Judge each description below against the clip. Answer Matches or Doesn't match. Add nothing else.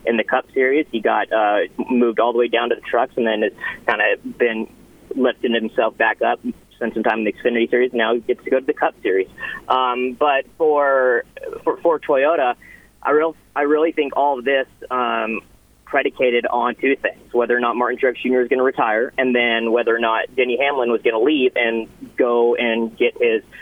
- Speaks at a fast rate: Matches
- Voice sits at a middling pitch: Doesn't match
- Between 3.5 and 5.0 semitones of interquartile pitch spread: Matches